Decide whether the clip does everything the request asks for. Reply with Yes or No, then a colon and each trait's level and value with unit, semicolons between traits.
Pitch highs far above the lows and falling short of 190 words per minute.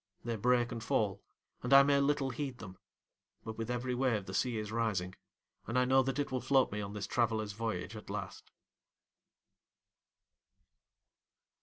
No: average, 3.3 semitones; average, 165 wpm